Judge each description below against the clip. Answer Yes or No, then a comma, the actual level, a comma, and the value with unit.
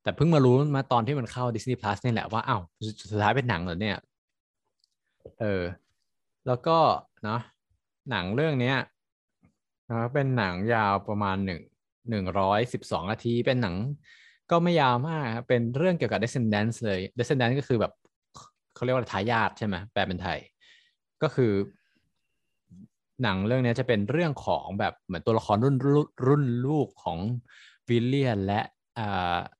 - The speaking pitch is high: No, low, 120 Hz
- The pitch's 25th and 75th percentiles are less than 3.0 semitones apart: No, average, 4.5 semitones